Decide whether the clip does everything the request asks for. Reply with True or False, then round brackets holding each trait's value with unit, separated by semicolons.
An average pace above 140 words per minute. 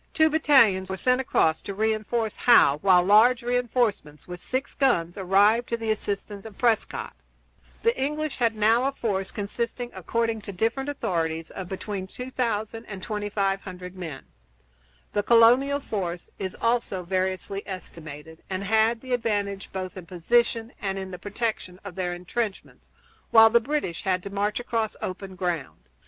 True (160 wpm)